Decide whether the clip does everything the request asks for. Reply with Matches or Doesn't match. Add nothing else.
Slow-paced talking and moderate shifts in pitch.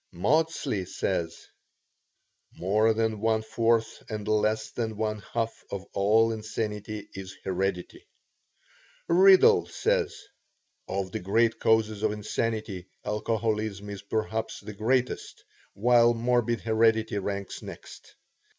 Doesn't match